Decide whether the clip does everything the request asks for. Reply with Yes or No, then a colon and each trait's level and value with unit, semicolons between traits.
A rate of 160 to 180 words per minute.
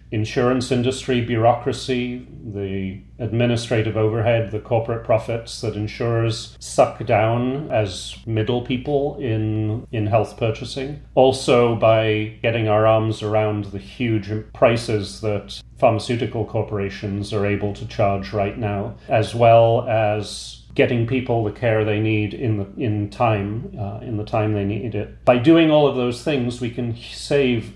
No: average, 145 wpm